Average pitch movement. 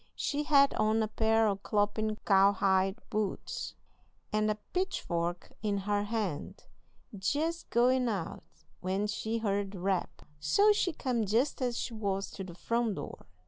Yes: average, 3.3 semitones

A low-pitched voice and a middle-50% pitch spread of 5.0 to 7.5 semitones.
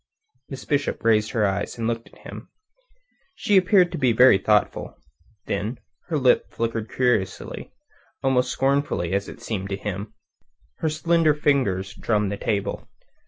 Yes: low, 115 Hz; wide, 5.6 semitones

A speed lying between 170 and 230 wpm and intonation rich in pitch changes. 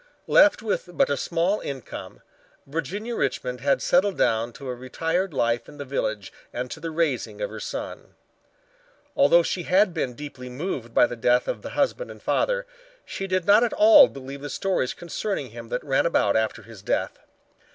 Yes: average, 185 wpm; wide, 7.7 semitones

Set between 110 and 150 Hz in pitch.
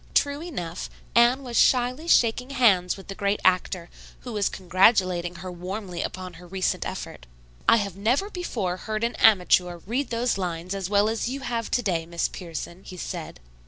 No: high, 200 Hz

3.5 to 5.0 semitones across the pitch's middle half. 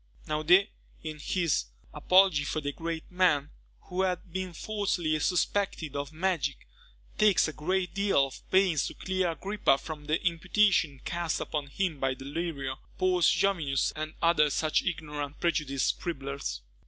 Yes: average, 4.1 semitones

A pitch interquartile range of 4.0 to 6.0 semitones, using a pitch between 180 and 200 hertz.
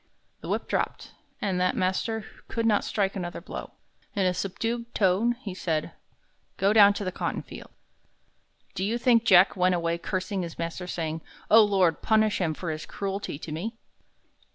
No: average, 3.4 semitones; high, 190 Hz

